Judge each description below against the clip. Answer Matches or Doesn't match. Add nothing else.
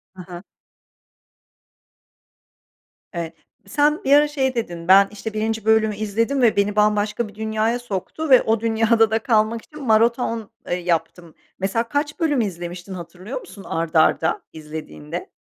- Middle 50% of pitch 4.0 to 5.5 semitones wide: Matches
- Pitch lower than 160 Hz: Doesn't match